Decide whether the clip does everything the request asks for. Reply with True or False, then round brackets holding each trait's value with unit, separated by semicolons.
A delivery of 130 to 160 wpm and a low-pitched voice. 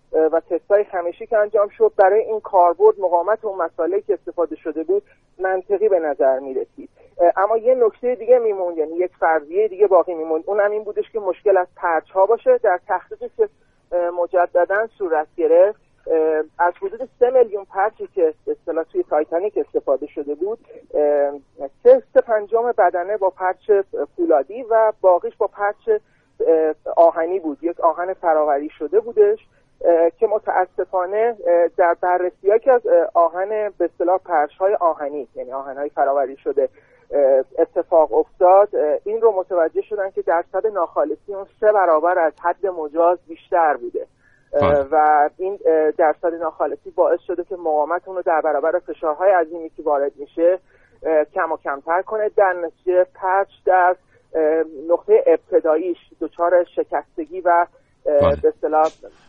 False (140 wpm; 185 Hz)